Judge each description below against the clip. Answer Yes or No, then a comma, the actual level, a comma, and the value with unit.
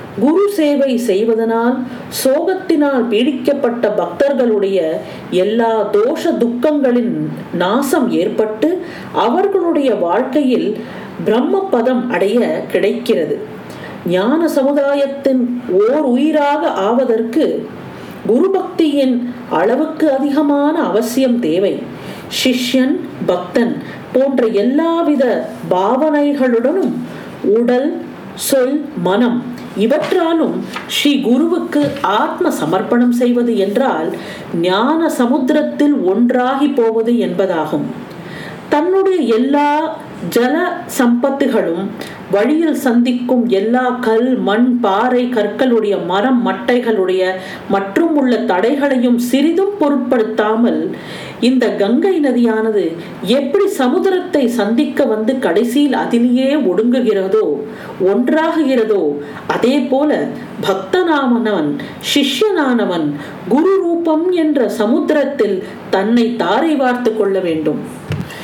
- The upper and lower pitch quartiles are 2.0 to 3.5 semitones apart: No, average, 4.6 semitones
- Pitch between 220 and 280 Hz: Yes, very high, 255 Hz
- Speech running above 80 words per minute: No, slow, 75 wpm